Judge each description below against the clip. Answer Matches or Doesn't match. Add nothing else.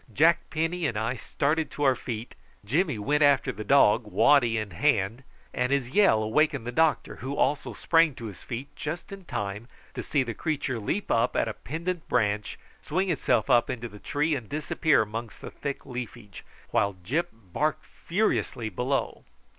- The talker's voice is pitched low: Matches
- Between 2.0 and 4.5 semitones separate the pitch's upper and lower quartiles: Doesn't match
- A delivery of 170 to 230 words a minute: Matches